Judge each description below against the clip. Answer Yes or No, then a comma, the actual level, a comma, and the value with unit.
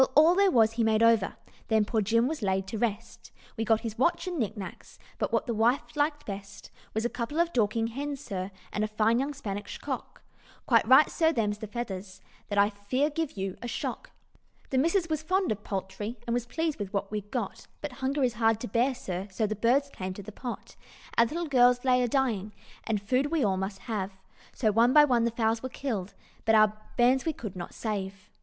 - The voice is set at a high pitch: Yes, high, 230 Hz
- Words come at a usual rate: No, fast, 220 wpm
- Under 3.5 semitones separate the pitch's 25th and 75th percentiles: No, average, 4.3 semitones